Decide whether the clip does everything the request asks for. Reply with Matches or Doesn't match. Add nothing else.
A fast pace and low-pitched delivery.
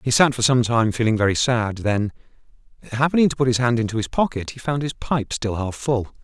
Matches